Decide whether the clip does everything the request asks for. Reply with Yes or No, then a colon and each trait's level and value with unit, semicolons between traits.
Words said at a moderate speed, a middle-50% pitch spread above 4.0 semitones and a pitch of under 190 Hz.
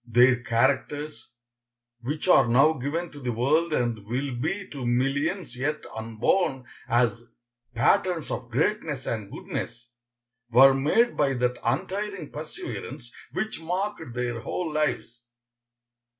No: slow, 120 wpm; average, 4.8 semitones; low, 135 Hz